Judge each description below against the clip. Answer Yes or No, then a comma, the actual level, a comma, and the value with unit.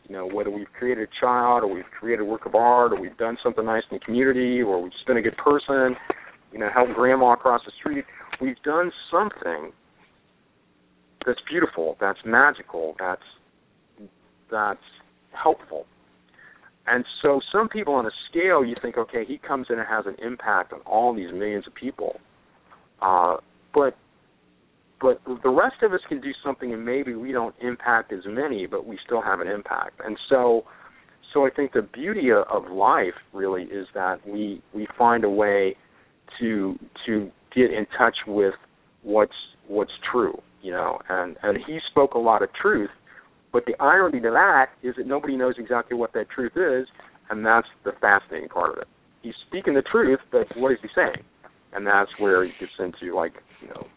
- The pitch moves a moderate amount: Yes, average, 4.1 semitones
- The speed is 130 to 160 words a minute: No, average, 185 wpm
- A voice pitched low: Yes, low, 120 Hz